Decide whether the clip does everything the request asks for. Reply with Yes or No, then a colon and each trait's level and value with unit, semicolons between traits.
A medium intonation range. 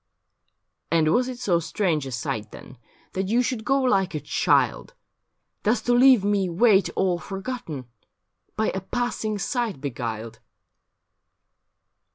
No: wide, 7.3 semitones